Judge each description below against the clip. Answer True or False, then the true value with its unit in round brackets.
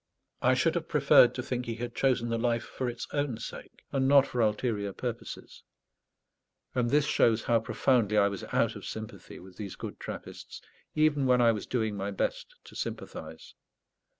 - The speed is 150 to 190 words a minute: True (180 wpm)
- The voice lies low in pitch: True (120 Hz)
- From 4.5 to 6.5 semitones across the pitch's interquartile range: False (3.2 semitones)